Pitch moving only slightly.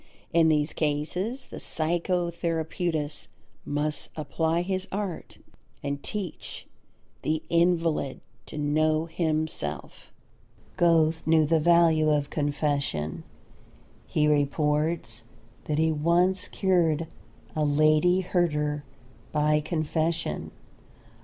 Yes: narrow, 2.2 semitones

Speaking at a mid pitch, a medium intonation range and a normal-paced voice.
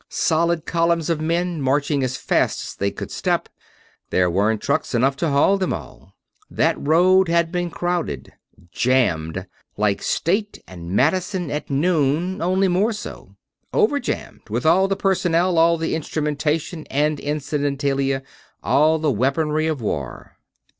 Yes: medium, 155 Hz; average, 4.4 semitones; average, 145 wpm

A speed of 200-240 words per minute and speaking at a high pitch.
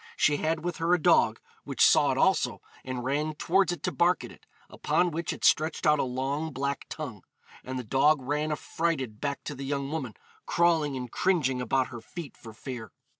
No: fast, 205 wpm; medium, 145 Hz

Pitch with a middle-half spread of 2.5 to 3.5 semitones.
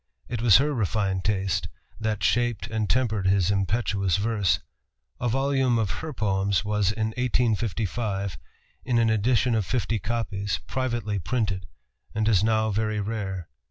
Yes: average, 3.0 semitones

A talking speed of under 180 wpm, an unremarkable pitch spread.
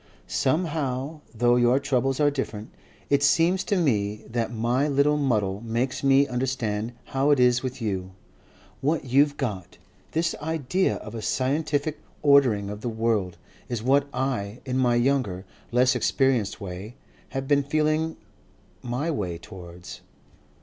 Yes: average, 145 wpm; average, 4.4 semitones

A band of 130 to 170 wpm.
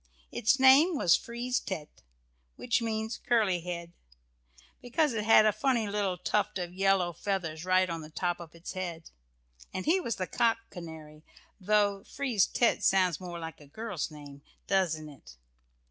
Yes: average, 160 wpm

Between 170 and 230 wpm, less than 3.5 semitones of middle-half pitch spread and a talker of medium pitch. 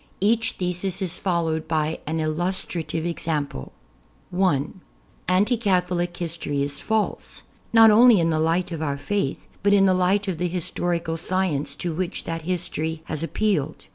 No: average, 155 wpm; average, 3.0 semitones; medium, 175 Hz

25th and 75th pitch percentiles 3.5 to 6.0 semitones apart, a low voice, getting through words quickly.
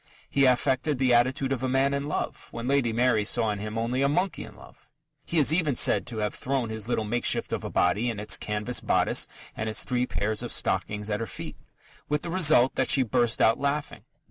Yes: average, 3.9 semitones; low, 125 Hz; fast, 225 wpm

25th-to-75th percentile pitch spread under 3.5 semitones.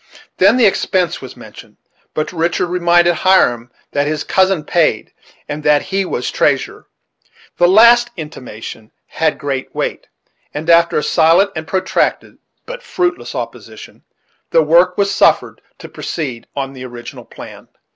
No: average, 4.5 semitones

